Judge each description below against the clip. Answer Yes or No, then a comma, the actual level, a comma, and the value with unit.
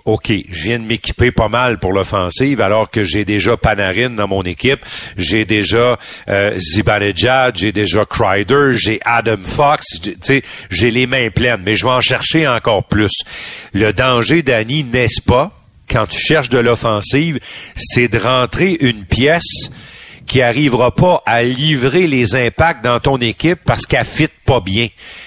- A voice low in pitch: Yes, low, 120 Hz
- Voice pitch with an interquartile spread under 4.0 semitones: Yes, average, 3.5 semitones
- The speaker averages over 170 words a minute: No, average, 165 wpm